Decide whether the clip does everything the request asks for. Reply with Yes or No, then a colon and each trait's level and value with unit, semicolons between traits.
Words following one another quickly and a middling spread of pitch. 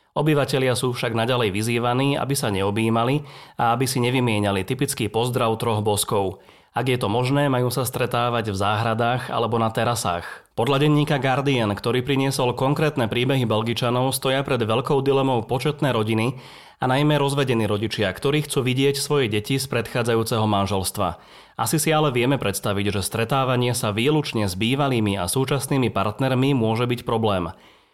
No: average, 155 wpm; average, 3.5 semitones